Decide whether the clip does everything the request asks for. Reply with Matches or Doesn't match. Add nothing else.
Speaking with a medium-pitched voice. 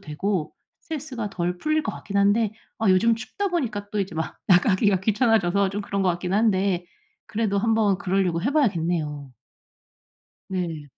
Doesn't match